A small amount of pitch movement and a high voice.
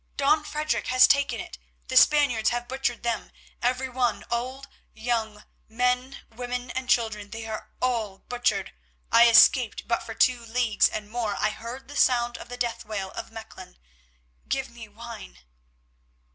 Yes: narrow, 2.3 semitones; high, 240 Hz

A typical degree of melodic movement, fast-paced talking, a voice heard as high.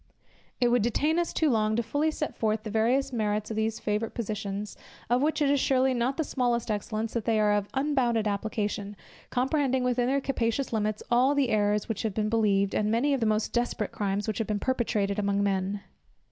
Yes: average, 3.4 semitones; fast, 210 wpm; high, 225 Hz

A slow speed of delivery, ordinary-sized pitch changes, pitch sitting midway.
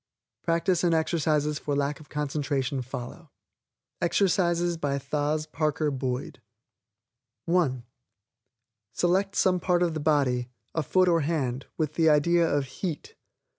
Yes: slow, 130 wpm; average, 3.2 semitones; medium, 155 Hz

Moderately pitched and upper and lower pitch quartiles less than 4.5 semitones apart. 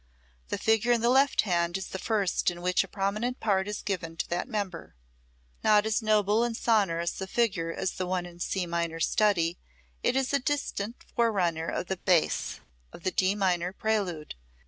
No: high, 195 Hz; average, 3.9 semitones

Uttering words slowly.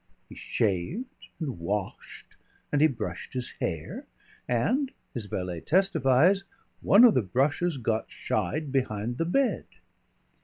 Yes: slow, 125 wpm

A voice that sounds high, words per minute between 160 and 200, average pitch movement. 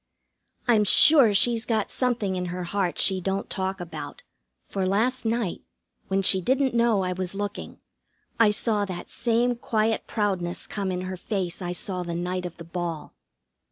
Yes: high, 195 Hz; average, 170 wpm; average, 3.7 semitones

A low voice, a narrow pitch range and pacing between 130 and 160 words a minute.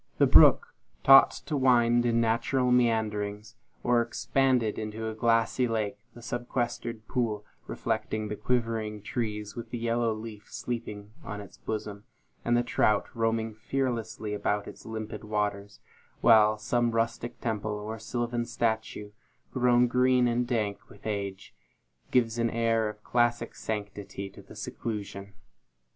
Yes: low, 115 Hz; narrow, 2.1 semitones; average, 140 wpm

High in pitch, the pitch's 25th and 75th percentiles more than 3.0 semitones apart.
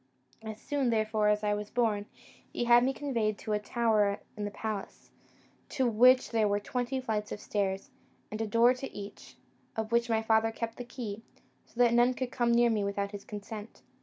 No: high, 220 Hz; narrow, 2.4 semitones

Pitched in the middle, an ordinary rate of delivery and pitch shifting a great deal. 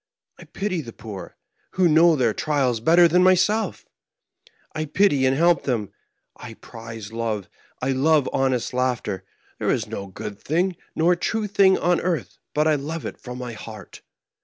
Yes: medium, 145 Hz; average, 165 wpm; wide, 6.9 semitones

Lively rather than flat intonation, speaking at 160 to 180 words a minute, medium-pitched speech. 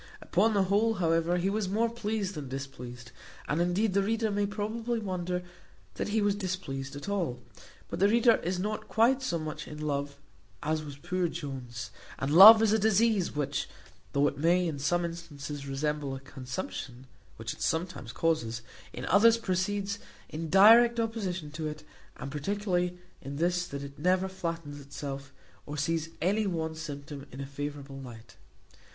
Yes: wide, 6.1 semitones; average, 170 wpm; medium, 170 Hz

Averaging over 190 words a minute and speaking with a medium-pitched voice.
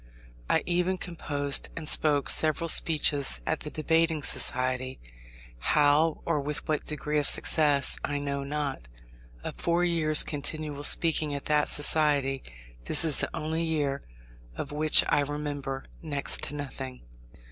No: average, 140 wpm; medium, 150 Hz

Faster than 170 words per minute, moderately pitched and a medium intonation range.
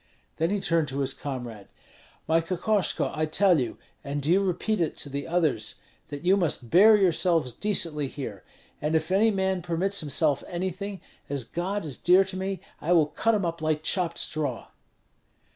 Yes: average, 180 wpm; medium, 165 Hz; average, 4.5 semitones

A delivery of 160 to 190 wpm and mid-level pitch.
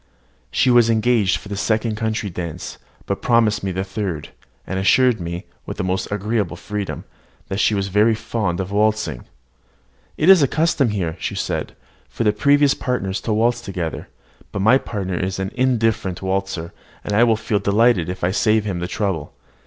No: average, 180 wpm; low, 105 Hz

